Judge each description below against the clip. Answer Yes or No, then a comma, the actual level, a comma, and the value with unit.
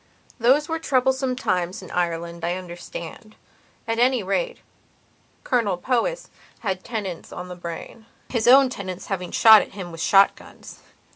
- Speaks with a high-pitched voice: Yes, high, 200 Hz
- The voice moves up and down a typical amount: No, wide, 6.0 semitones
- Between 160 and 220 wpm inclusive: No, average, 145 wpm